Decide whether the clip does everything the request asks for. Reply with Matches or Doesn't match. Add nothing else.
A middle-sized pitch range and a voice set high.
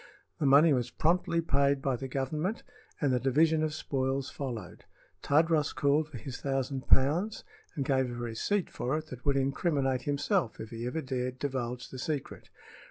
Doesn't match